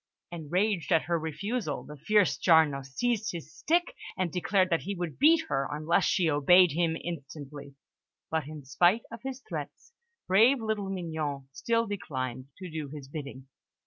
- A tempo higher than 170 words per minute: No, average, 160 wpm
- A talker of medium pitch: Yes, medium, 170 Hz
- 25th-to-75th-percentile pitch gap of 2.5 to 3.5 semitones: No, wide, 5.6 semitones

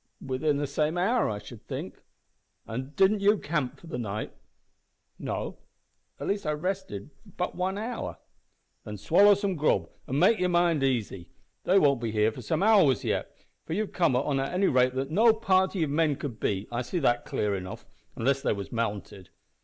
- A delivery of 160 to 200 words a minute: Yes, average, 190 wpm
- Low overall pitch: No, medium, 150 Hz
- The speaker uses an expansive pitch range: Yes, wide, 7.4 semitones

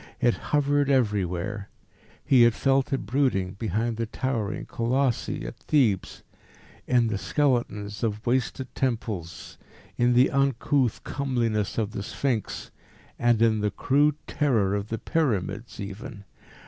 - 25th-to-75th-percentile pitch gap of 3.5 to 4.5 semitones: Yes, average, 4.2 semitones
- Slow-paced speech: Yes, slow, 130 wpm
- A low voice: Yes, low, 120 Hz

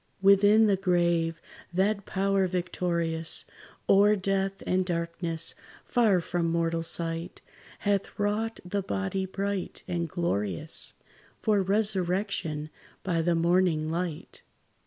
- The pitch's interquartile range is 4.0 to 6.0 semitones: No, average, 2.9 semitones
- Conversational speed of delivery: No, slow, 110 wpm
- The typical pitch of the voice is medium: Yes, medium, 180 Hz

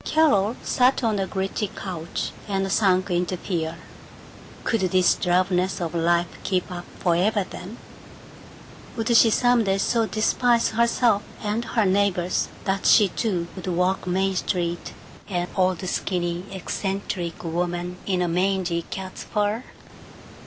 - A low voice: No, high, 190 Hz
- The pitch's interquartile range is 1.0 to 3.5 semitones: Yes, average, 2.8 semitones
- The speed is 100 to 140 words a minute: Yes, slow, 135 wpm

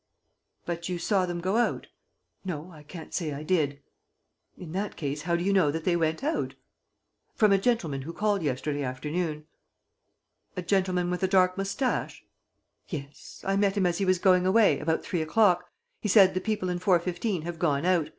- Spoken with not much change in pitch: No, average, 3.4 semitones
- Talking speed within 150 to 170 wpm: No, average, 190 wpm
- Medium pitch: Yes, medium, 180 Hz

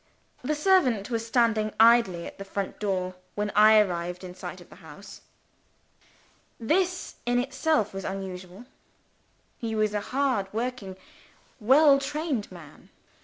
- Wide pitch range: No, average, 4.9 semitones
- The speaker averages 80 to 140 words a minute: Yes, slow, 135 wpm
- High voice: Yes, high, 220 Hz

